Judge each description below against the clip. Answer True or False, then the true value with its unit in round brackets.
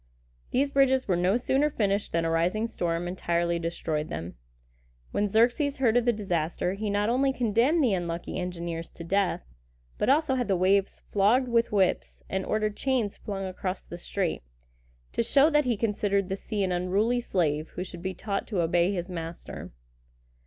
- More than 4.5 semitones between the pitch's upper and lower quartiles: True (5.0 semitones)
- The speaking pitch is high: True (200 Hz)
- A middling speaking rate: True (180 wpm)